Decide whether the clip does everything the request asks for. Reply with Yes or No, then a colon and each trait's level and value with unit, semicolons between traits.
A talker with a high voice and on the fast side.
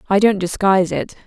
No: high, 195 Hz; average, 190 wpm